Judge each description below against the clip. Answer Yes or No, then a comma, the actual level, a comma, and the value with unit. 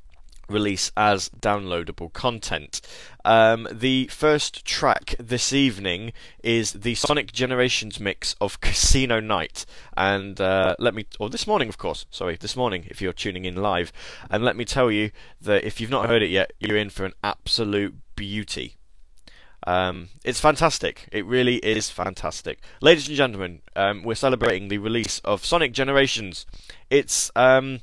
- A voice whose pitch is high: No, low, 105 Hz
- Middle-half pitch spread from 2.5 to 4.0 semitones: No, average, 4.6 semitones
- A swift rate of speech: No, average, 155 wpm